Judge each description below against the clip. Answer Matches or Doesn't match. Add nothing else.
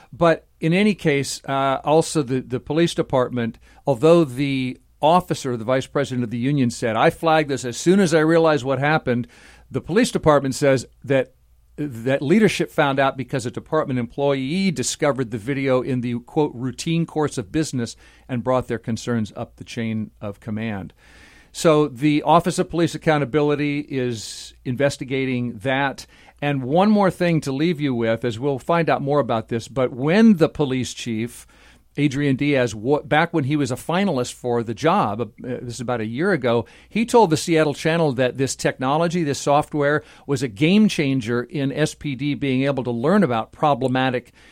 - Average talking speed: Matches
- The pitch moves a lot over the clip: Doesn't match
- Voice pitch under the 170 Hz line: Matches